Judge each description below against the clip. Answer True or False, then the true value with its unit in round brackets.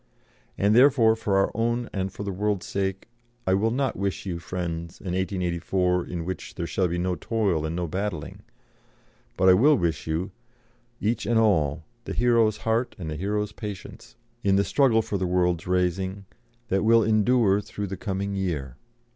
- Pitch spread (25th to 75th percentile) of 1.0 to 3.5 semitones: True (3.2 semitones)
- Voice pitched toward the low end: True (95 Hz)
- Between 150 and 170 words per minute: False (180 wpm)